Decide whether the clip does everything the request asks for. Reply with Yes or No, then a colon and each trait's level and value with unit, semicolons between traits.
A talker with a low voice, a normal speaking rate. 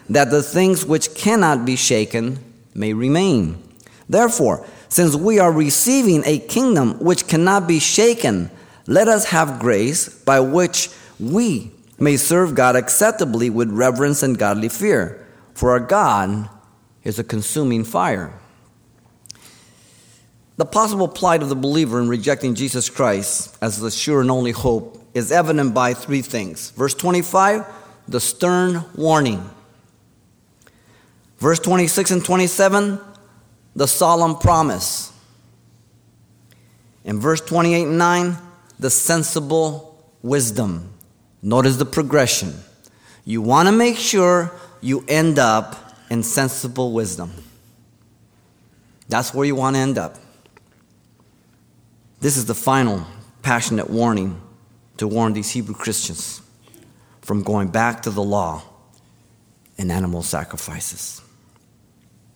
No: low, 130 Hz; slow, 120 wpm